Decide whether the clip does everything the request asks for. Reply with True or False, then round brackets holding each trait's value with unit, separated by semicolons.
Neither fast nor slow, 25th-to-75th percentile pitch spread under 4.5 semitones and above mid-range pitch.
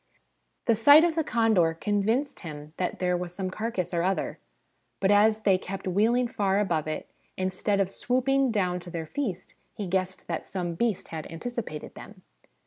True (175 wpm; 4.1 semitones; 195 Hz)